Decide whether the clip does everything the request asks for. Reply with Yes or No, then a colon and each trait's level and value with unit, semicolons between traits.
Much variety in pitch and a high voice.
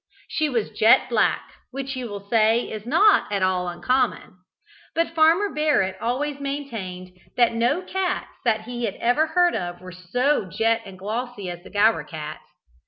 Yes: wide, 6.7 semitones; high, 230 Hz